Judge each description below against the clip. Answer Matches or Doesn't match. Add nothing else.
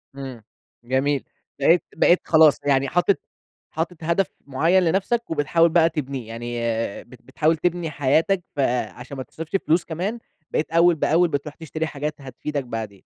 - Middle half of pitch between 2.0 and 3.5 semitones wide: Doesn't match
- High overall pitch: Doesn't match